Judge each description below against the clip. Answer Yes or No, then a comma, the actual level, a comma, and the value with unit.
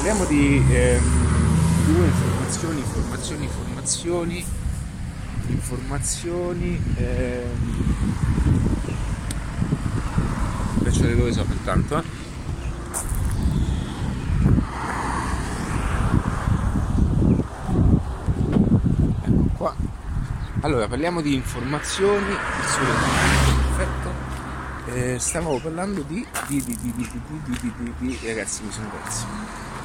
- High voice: No, low, 120 Hz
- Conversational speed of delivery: No, slow, 75 wpm